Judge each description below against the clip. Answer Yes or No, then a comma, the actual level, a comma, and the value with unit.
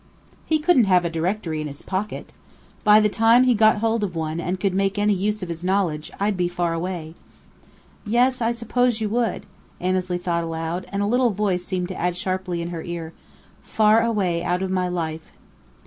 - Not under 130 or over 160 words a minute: No, average, 200 wpm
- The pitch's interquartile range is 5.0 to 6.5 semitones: No, average, 3.7 semitones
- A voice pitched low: No, medium, 185 Hz